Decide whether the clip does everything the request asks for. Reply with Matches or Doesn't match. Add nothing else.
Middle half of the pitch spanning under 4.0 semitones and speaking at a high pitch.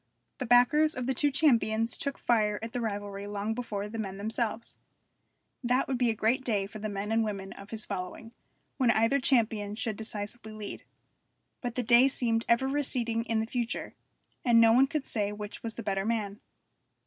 Matches